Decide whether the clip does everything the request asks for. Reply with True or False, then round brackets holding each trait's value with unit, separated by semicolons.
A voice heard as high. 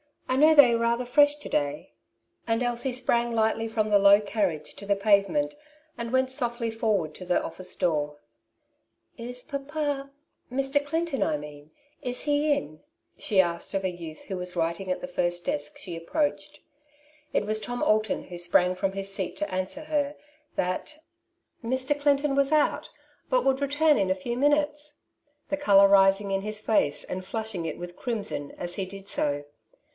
True (220 Hz)